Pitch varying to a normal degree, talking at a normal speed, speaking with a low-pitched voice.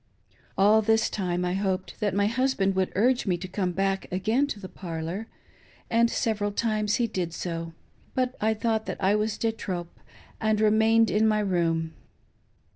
No: average, 3.1 semitones; average, 175 wpm; high, 205 Hz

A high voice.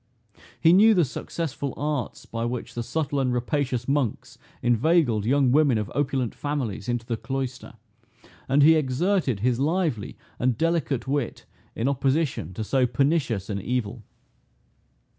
No: low, 130 Hz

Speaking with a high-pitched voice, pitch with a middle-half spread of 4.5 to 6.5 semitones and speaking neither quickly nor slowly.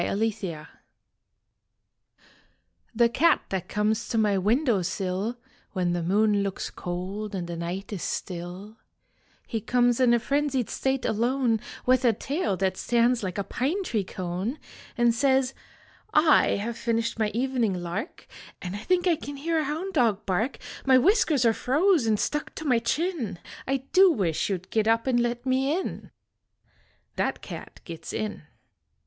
Yes: high, 230 Hz; average, 5.2 semitones; average, 165 wpm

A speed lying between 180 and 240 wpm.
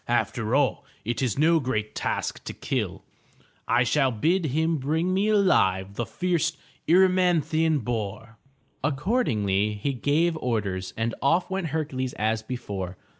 No: average, 150 wpm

